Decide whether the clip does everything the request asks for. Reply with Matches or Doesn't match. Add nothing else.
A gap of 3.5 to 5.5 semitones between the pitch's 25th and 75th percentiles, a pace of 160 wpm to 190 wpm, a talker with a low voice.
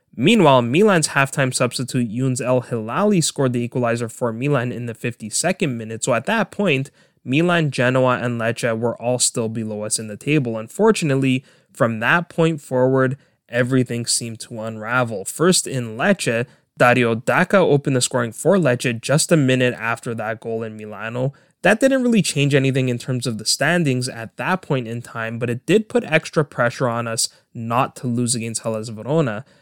Matches